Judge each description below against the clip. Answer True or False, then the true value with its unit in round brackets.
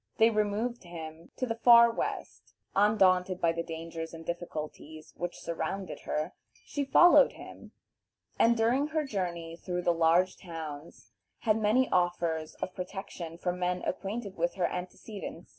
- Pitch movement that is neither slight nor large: True (4.3 semitones)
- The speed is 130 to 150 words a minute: True (145 wpm)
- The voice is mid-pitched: True (180 Hz)